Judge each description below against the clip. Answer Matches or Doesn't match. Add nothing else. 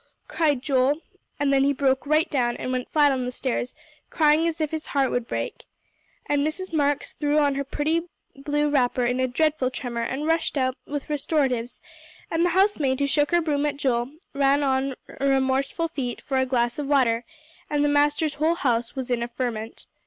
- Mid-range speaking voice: Doesn't match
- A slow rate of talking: Doesn't match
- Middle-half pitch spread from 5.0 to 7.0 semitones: Doesn't match